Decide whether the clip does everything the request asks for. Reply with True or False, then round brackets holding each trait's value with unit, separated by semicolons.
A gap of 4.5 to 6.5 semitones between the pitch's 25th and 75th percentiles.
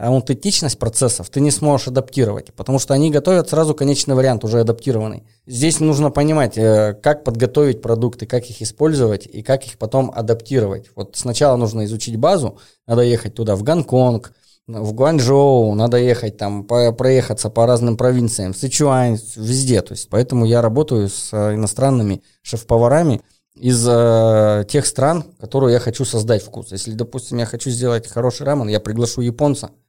False (3.3 semitones)